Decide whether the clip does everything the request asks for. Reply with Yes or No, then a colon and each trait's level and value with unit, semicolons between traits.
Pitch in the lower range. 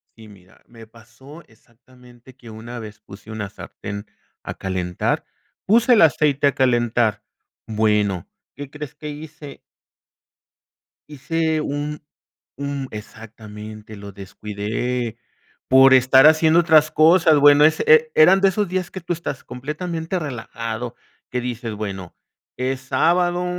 Yes: low, 130 Hz